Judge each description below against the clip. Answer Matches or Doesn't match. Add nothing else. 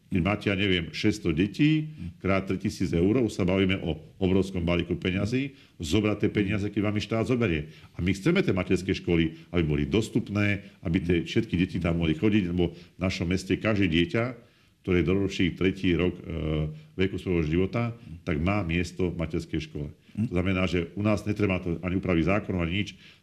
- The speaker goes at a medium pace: Doesn't match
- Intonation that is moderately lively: Matches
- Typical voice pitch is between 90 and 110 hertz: Matches